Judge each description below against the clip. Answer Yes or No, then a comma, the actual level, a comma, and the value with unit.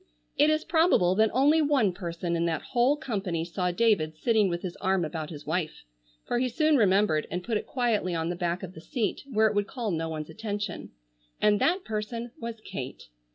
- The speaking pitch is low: No, high, 195 Hz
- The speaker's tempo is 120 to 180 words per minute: No, average, 200 wpm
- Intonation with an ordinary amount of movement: No, wide, 5.7 semitones